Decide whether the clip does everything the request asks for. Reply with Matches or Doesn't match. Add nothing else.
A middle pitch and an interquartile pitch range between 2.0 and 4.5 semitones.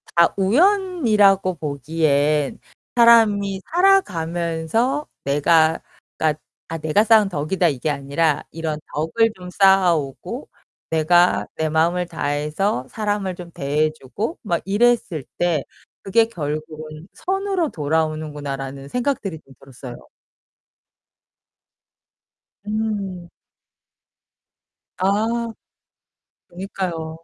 Doesn't match